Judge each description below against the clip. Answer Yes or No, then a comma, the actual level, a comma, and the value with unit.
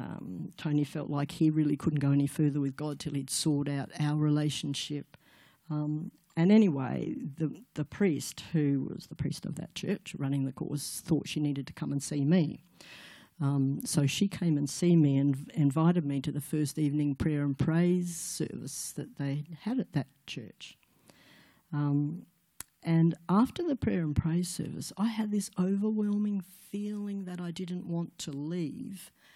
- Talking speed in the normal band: Yes, average, 175 wpm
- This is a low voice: No, medium, 155 Hz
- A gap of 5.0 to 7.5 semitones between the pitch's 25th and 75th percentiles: No, average, 3.7 semitones